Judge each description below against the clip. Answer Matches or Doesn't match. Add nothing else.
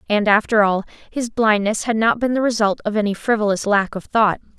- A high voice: Matches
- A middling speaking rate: Doesn't match